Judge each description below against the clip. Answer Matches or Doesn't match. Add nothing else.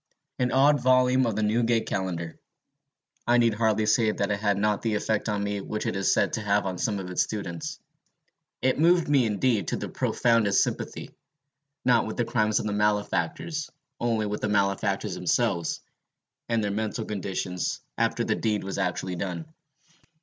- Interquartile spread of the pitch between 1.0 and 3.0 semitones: Matches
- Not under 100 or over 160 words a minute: Doesn't match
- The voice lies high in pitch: Doesn't match